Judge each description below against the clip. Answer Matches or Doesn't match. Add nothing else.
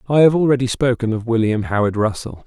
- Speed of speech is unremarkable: Matches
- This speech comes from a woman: Doesn't match